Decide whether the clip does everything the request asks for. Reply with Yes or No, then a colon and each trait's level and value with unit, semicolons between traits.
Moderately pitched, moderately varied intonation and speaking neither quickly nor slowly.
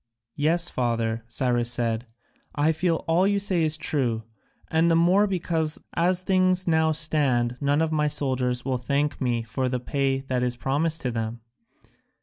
Yes: medium, 145 Hz; average, 4.9 semitones; average, 160 wpm